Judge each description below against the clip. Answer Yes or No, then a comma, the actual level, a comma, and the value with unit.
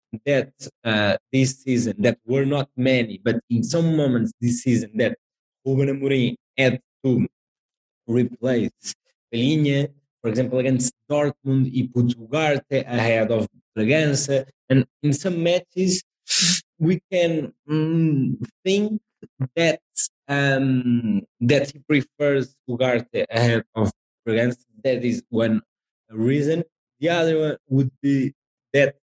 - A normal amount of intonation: Yes, average, 3.4 semitones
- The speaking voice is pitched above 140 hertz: No, low, 135 Hz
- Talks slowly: Yes, slow, 120 wpm